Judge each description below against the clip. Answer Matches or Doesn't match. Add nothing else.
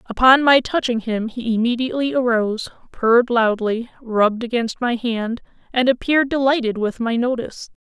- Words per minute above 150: Doesn't match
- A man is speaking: Doesn't match